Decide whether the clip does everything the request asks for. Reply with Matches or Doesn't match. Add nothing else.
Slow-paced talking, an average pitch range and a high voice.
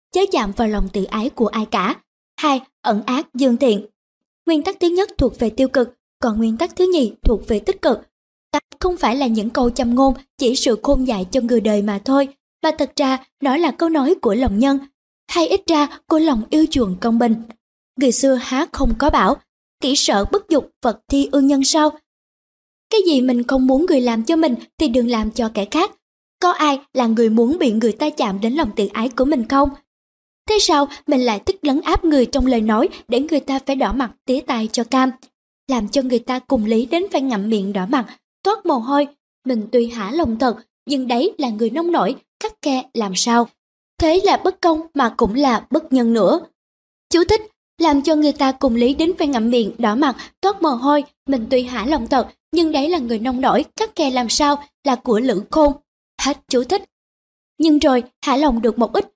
Doesn't match